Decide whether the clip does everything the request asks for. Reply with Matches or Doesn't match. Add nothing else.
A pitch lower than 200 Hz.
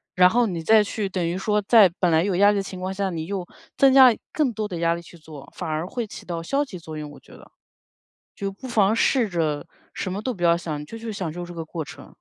Matches